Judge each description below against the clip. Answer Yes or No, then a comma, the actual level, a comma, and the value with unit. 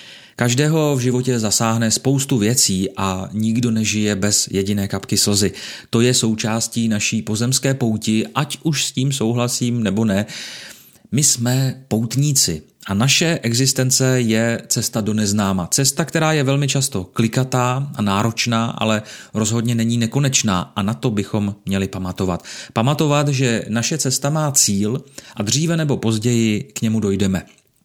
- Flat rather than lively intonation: No, average, 3.9 semitones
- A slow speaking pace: No, average, 145 wpm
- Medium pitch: No, low, 115 Hz